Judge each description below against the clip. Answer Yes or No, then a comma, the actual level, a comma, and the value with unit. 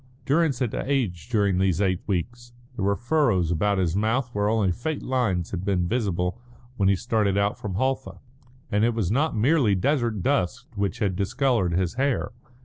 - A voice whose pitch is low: Yes, low, 105 Hz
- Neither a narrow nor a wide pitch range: Yes, average, 4.7 semitones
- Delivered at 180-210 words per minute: Yes, average, 185 wpm